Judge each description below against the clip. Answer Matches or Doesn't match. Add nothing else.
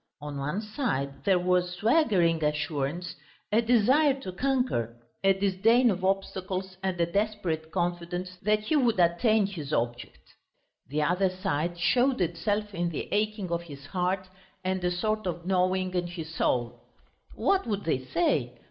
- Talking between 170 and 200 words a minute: Doesn't match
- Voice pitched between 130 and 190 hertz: Matches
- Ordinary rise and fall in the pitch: Matches